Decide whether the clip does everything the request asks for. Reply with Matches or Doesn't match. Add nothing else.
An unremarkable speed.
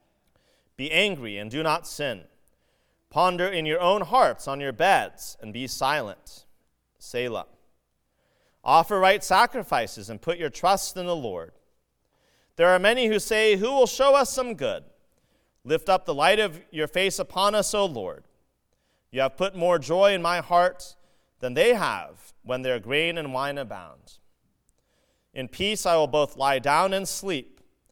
Matches